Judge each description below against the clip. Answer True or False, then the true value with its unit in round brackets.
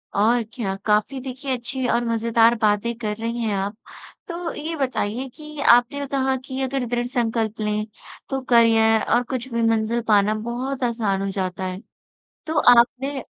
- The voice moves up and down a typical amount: True (3.2 semitones)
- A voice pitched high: True (235 Hz)